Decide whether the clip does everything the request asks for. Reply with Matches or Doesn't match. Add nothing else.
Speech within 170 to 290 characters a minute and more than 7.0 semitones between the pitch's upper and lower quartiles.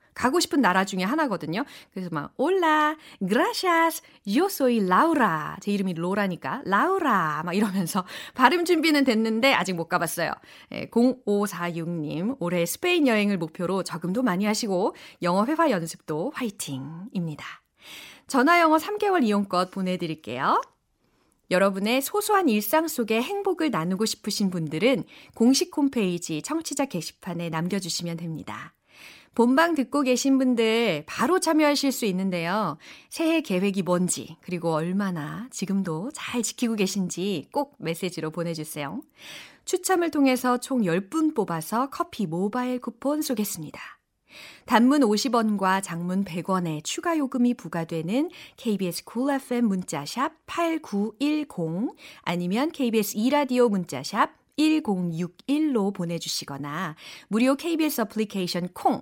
Doesn't match